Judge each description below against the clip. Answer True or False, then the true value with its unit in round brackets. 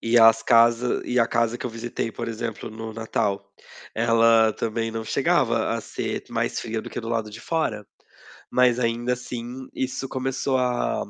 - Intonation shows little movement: True (1.6 semitones)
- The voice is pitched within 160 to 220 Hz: False (115 Hz)